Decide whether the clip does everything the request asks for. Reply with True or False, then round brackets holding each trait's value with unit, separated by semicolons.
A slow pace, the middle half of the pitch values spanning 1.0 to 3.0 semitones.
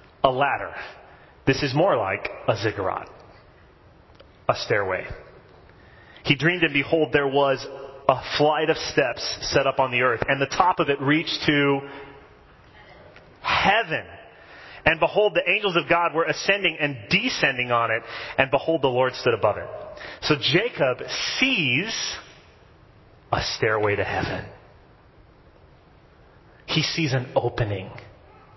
False (130 wpm; 5.1 semitones)